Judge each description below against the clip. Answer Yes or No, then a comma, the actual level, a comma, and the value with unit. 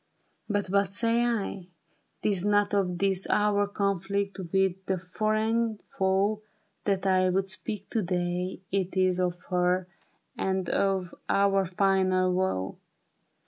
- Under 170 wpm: Yes, average, 140 wpm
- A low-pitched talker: No, high, 190 Hz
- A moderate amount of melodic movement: No, narrow, 1.6 semitones